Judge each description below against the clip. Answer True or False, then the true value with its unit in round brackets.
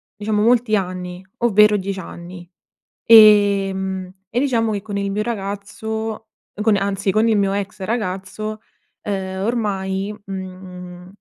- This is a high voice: True (200 Hz)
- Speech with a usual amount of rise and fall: False (2.1 semitones)